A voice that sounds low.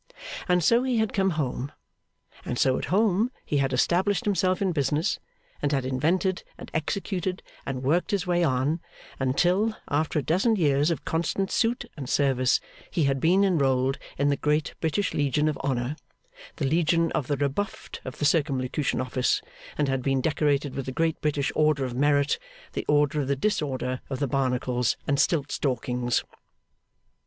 No: medium, 145 Hz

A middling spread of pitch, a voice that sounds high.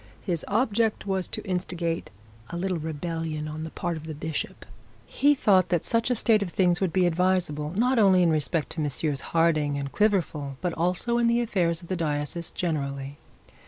No: average, 3.8 semitones; medium, 170 Hz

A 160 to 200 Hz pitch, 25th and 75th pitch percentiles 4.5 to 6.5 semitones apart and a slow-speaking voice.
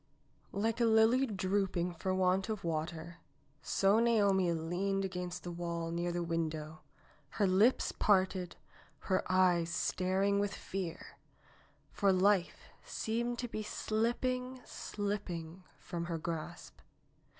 No: medium, 185 Hz; average, 3.3 semitones; slow, 120 wpm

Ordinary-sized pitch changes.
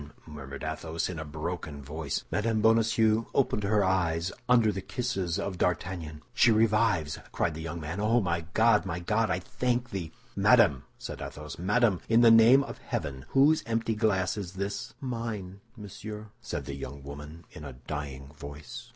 No: wide, 6.2 semitones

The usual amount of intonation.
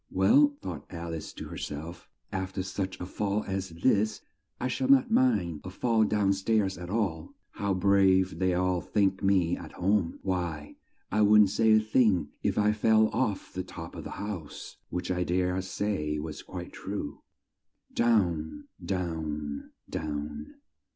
Yes: average, 3.6 semitones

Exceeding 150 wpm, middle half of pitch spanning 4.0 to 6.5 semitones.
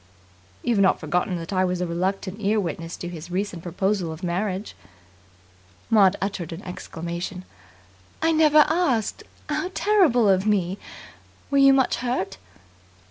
No: average, 140 wpm; average, 4.4 semitones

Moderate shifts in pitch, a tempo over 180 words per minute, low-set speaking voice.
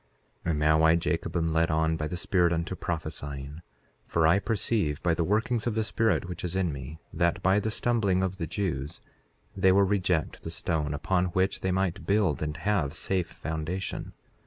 Yes: average, 3.2 semitones; average, 195 wpm; very low, 85 Hz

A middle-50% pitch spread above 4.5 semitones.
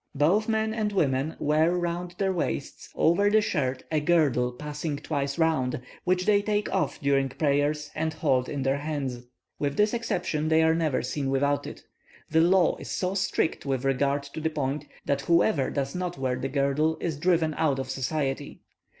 No: average, 3.8 semitones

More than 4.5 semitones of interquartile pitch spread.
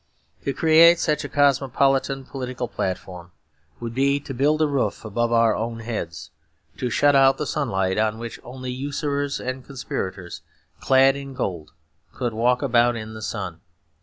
No: average, 3.8 semitones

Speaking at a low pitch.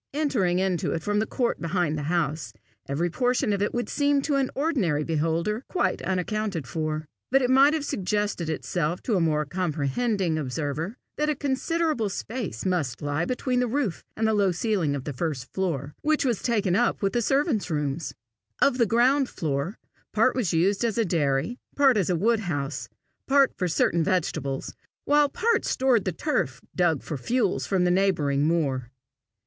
No: high, 190 Hz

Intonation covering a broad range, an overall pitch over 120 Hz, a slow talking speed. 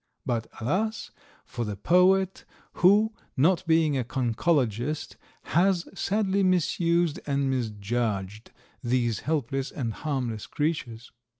Yes: wide, 6.8 semitones; medium, 140 Hz; slow, 105 wpm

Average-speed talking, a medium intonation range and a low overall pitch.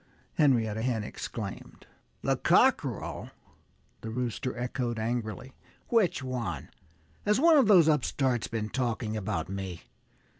No: slow, 115 wpm; average, 3.6 semitones; low, 120 Hz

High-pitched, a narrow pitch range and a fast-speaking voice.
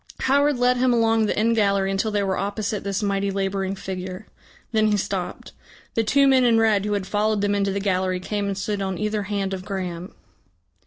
Yes: high, 200 Hz; narrow, 2.1 semitones; fast, 210 wpm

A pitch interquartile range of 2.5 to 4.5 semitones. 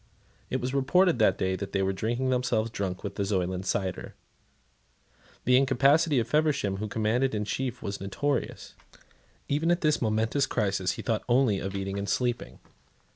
No: average, 5.2 semitones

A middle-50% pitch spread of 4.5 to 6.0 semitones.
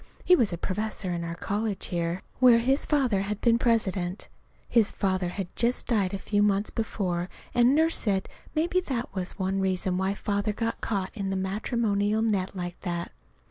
No: average, 3.5 semitones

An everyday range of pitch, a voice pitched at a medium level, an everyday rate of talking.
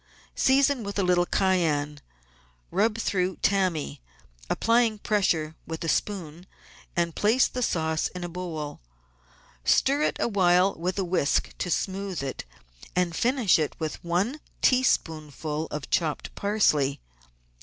No: average, 4.5 semitones; medium, 180 Hz; slow, 125 wpm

